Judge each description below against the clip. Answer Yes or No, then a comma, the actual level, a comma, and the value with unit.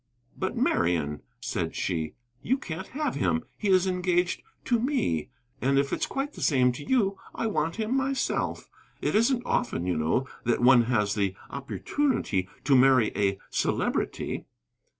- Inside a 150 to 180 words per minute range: Yes, average, 155 wpm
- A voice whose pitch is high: No, medium, 145 Hz